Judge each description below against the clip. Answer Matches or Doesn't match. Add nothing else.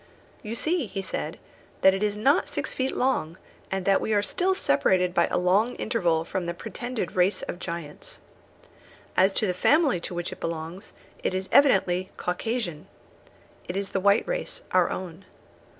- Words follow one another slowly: Doesn't match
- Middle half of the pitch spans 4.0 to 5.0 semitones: Matches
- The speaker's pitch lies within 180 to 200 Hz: Matches